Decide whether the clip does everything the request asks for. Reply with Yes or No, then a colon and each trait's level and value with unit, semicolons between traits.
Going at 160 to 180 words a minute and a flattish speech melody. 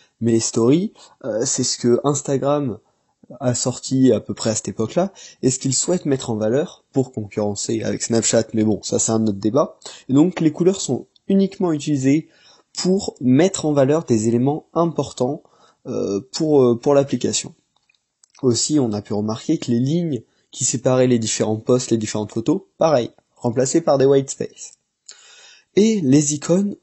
No: average, 175 wpm; average, 4.9 semitones